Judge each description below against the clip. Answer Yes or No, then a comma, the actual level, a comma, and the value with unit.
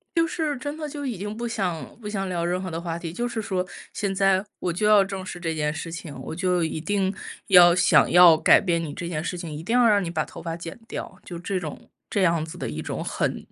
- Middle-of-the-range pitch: Yes, medium, 180 Hz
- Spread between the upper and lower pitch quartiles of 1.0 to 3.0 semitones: No, average, 3.5 semitones